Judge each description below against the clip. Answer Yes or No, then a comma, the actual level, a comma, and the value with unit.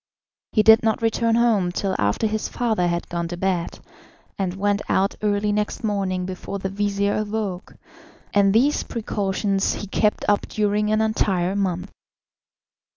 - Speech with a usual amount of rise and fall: No, narrow, 2.1 semitones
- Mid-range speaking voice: No, high, 205 Hz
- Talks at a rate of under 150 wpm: No, average, 155 wpm